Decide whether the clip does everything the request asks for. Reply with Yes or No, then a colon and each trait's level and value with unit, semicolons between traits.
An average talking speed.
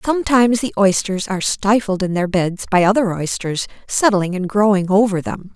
Yes: average, 175 wpm